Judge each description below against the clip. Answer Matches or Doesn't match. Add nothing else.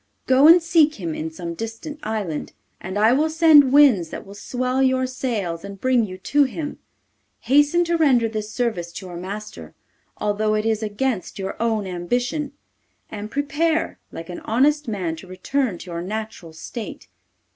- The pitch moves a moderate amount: Doesn't match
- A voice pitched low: Doesn't match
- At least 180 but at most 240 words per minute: Doesn't match